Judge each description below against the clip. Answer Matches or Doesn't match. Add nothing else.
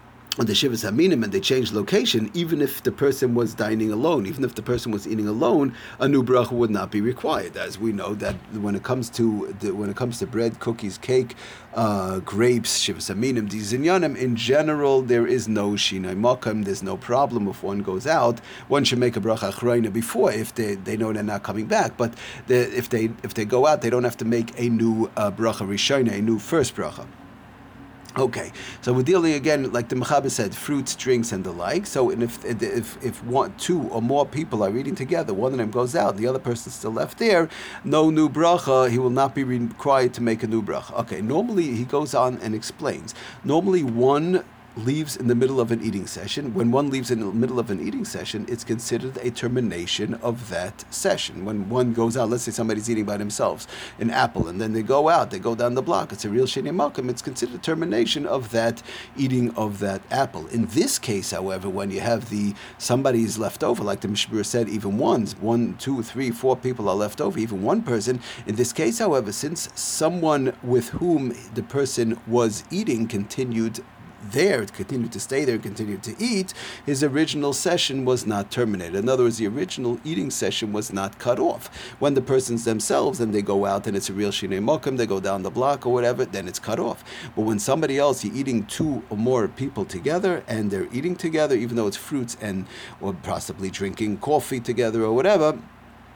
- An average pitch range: Matches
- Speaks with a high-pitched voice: Doesn't match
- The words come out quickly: Matches